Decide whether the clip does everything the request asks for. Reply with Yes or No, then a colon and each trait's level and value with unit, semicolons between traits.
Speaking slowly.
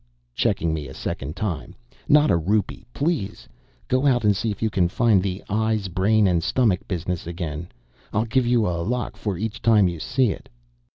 No: average, 190 wpm